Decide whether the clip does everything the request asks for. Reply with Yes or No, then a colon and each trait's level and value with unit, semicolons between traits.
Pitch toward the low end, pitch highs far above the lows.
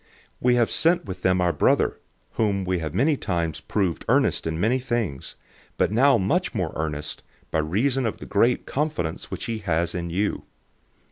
Yes: very low, 95 Hz; wide, 6.2 semitones